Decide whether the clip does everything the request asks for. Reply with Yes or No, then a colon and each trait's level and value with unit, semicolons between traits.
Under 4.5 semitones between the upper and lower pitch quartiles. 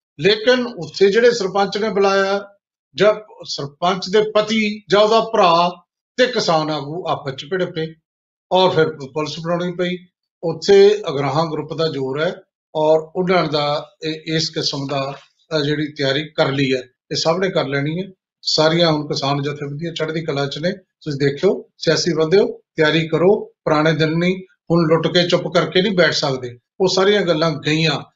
Yes: average, 3.8 semitones